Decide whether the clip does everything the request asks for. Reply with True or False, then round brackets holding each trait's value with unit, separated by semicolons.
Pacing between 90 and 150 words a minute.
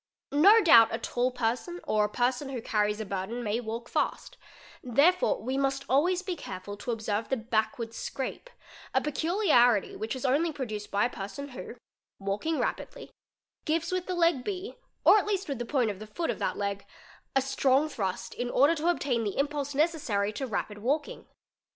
False (195 wpm)